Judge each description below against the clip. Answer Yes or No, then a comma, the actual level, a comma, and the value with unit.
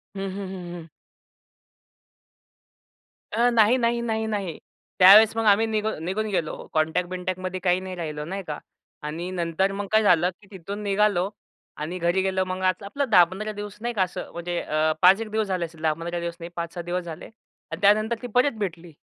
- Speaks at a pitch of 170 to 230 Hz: Yes, medium, 185 Hz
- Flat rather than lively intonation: No, average, 3.5 semitones